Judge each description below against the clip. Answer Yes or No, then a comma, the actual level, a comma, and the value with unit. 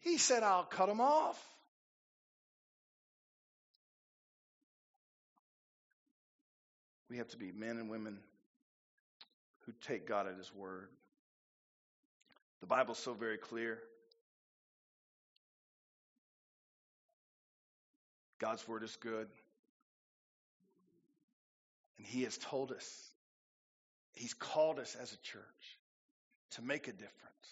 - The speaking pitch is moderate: Yes, medium, 155 Hz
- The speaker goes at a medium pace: No, slow, 95 wpm